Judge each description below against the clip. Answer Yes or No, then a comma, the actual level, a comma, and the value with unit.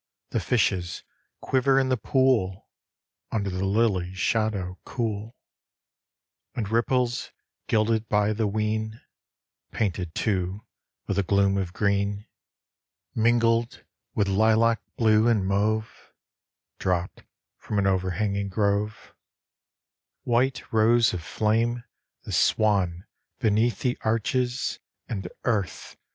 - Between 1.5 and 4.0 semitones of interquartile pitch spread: Yes, average, 2.7 semitones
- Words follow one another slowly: Yes, slow, 110 wpm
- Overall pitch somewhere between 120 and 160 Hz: No, low, 110 Hz